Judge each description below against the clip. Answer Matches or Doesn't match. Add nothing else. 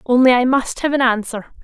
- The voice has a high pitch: Matches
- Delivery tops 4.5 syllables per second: Matches